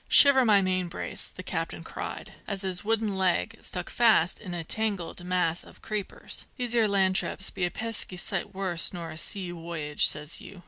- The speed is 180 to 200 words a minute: Yes, average, 190 wpm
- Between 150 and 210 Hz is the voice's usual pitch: Yes, high, 190 Hz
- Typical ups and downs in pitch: Yes, average, 3.4 semitones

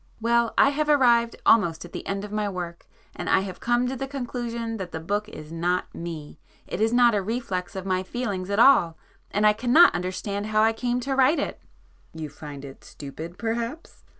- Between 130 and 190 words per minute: No, average, 200 wpm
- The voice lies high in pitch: Yes, high, 210 Hz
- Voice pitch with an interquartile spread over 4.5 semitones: Yes, average, 5.0 semitones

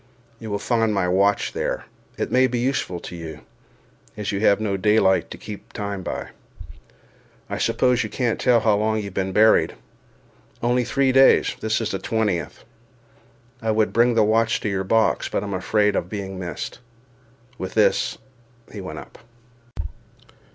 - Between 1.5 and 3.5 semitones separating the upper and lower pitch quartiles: Yes, average, 2.8 semitones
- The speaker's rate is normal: Yes, average, 160 wpm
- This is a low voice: Yes, low, 105 Hz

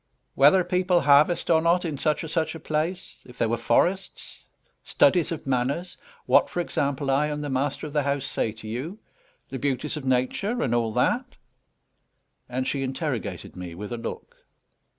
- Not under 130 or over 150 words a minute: No, average, 180 wpm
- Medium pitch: Yes, medium, 145 Hz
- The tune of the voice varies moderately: Yes, average, 4.6 semitones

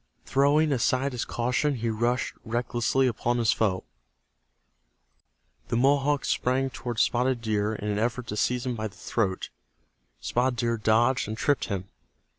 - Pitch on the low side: Yes, low, 120 Hz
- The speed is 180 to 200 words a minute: No, average, 150 wpm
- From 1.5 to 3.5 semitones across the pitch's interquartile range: Yes, average, 2.9 semitones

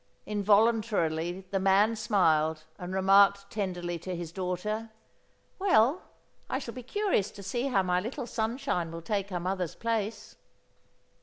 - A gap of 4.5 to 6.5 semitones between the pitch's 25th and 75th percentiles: No, average, 3.9 semitones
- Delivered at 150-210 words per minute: No, average, 140 wpm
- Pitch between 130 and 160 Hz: No, high, 200 Hz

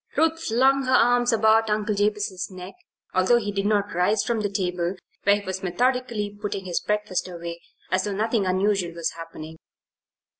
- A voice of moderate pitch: No, high, 205 Hz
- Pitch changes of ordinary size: Yes, average, 3.2 semitones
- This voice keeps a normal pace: Yes, average, 175 wpm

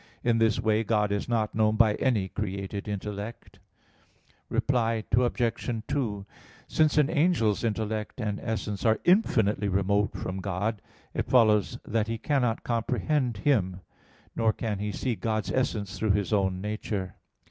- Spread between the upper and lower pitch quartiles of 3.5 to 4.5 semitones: No, narrow, 2.4 semitones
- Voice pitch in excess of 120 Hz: No, low, 110 Hz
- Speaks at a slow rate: No, average, 145 wpm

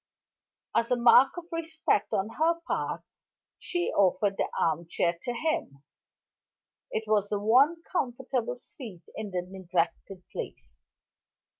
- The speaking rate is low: Yes, slow, 125 wpm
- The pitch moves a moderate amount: No, wide, 6.3 semitones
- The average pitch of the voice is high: Yes, high, 225 Hz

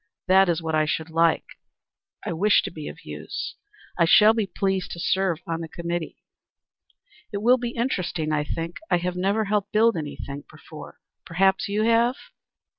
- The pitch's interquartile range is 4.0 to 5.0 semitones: Yes, average, 4.3 semitones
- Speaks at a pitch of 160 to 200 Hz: Yes, medium, 185 Hz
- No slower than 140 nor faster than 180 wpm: Yes, average, 175 wpm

